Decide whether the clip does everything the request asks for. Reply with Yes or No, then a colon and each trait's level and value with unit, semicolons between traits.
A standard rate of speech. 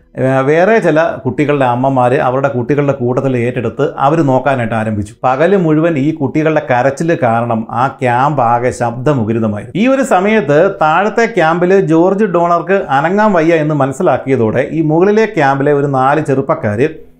No: fast, 135 wpm